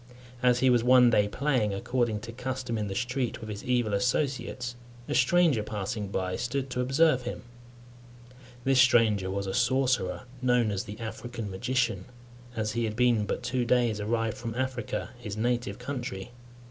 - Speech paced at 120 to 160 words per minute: No, average, 170 wpm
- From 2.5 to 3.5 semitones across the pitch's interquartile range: Yes, average, 3.0 semitones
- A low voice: Yes, low, 120 Hz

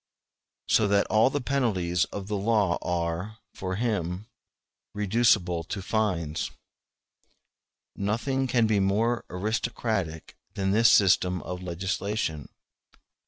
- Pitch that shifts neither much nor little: Yes, average, 3.5 semitones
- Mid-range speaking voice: No, low, 100 Hz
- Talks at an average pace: No, slow, 115 wpm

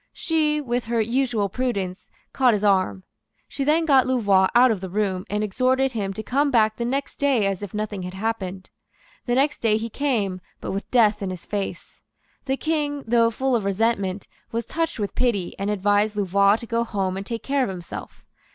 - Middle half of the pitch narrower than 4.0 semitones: No, average, 4.5 semitones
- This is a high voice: Yes, high, 220 Hz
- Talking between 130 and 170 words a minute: No, average, 200 wpm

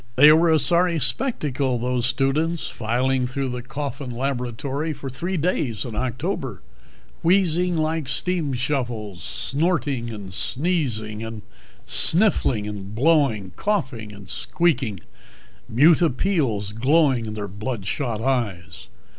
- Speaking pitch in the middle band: No, low, 130 Hz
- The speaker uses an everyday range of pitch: No, wide, 5.7 semitones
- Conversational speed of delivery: No, slow, 120 wpm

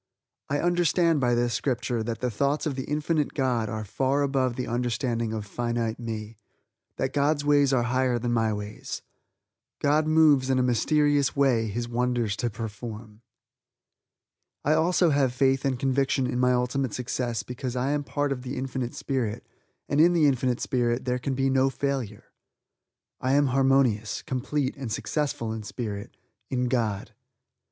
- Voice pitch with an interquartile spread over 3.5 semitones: No, average, 2.9 semitones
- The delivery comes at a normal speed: Yes, average, 165 wpm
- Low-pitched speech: Yes, low, 130 Hz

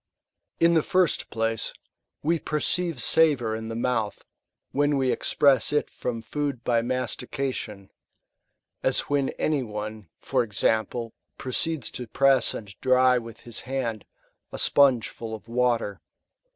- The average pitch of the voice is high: No, low, 125 Hz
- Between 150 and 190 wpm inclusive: No, slow, 135 wpm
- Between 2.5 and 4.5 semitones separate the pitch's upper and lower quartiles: Yes, average, 3.8 semitones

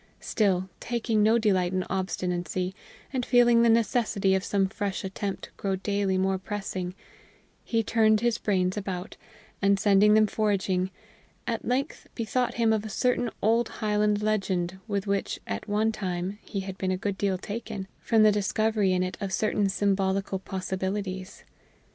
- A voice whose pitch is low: No, high, 200 Hz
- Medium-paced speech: Yes, average, 160 wpm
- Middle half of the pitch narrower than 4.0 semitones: Yes, narrow, 2.4 semitones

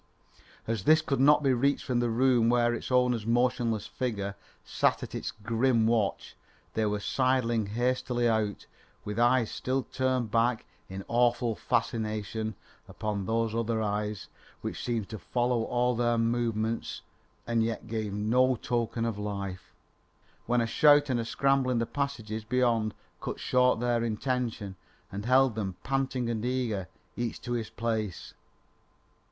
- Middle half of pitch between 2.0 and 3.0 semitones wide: Yes, narrow, 2.4 semitones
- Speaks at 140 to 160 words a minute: Yes, average, 150 wpm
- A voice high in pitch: No, low, 115 Hz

